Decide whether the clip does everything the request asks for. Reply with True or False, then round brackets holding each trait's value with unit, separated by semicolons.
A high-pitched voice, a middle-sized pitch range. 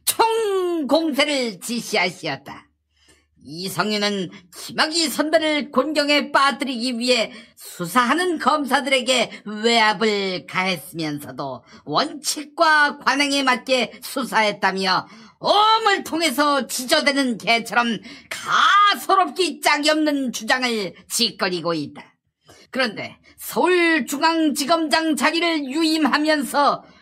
False (265 Hz; 6.5 semitones)